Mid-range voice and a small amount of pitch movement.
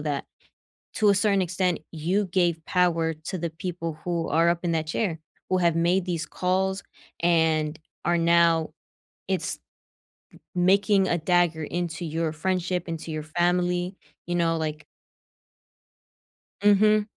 Yes: medium, 175 Hz; narrow, 2.1 semitones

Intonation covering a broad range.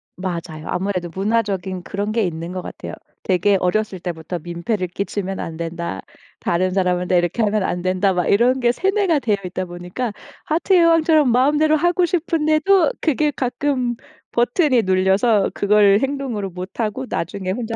Yes: wide, 6.3 semitones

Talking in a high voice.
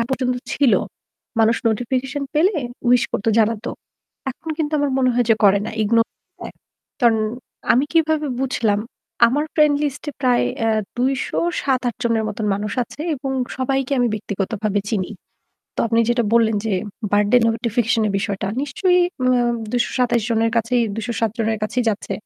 Yes: high, 240 Hz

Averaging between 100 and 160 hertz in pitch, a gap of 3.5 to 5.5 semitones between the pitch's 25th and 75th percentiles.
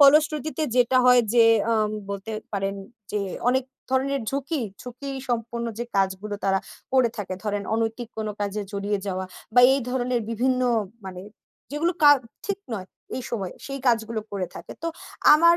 No: high, 235 Hz; average, 4.6 semitones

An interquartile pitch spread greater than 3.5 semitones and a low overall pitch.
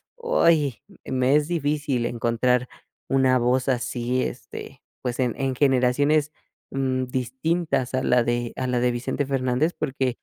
No: narrow, 2.5 semitones; low, 130 Hz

